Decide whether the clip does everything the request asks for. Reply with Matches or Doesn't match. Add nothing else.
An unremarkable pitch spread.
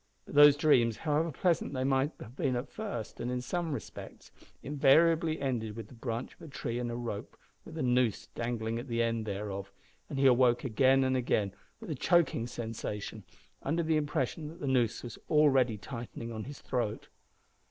Matches